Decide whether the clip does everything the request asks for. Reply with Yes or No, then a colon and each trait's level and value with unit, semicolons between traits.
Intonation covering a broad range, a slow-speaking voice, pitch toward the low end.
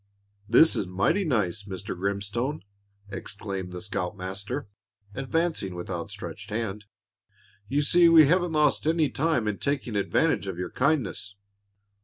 Yes: wide, 7.4 semitones; slow, 130 wpm; low, 105 Hz